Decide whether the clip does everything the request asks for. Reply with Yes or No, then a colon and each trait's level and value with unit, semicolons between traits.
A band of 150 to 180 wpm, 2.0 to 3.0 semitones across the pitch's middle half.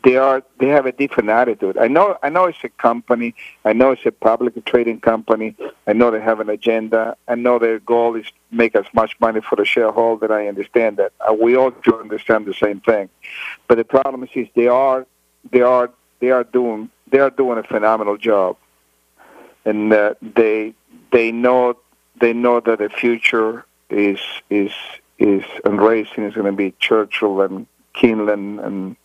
No: average, 190 wpm; narrow, 2.6 semitones